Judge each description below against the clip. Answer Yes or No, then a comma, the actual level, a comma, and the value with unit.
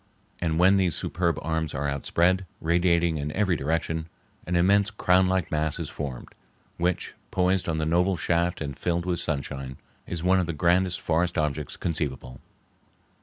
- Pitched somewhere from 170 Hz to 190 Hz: No, very low, 85 Hz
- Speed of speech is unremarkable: Yes, average, 160 wpm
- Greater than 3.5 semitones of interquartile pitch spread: No, average, 2.7 semitones